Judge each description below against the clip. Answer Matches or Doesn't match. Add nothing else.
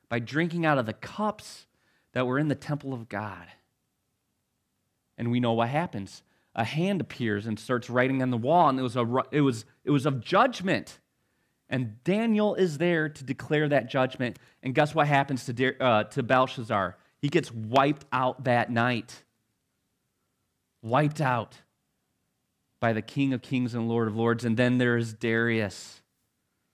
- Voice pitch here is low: Matches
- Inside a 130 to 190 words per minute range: Matches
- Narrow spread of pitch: Doesn't match